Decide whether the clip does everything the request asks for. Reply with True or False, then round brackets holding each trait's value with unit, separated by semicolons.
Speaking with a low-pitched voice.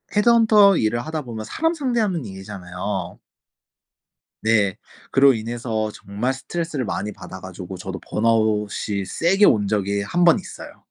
True (110 Hz)